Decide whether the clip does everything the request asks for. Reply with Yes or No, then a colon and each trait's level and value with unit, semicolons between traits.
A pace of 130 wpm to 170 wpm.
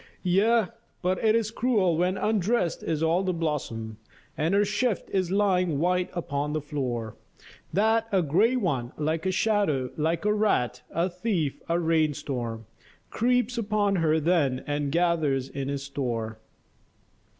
Yes: average, 150 wpm